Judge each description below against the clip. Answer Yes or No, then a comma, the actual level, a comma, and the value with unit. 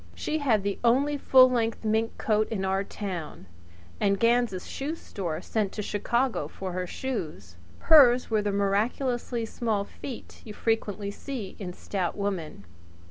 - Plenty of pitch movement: No, average, 3.7 semitones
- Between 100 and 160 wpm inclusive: Yes, average, 150 wpm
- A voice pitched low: No, high, 215 Hz